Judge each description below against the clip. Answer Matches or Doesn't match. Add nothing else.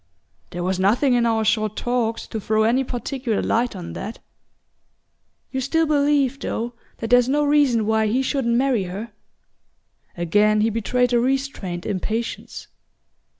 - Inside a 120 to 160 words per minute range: Matches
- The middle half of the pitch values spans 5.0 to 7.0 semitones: Doesn't match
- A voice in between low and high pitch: Doesn't match